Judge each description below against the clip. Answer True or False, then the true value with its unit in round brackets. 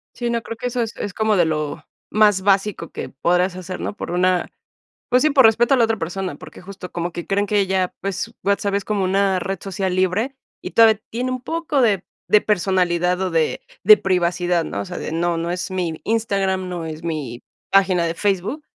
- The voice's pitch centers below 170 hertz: False (190 Hz)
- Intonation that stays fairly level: False (3.4 semitones)